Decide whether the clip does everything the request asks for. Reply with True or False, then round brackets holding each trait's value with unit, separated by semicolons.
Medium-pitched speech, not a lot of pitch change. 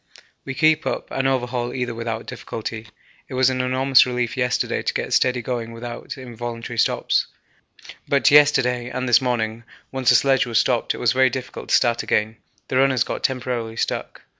False (125 Hz; 1.8 semitones)